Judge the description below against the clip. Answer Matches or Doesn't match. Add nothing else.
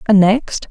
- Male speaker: Doesn't match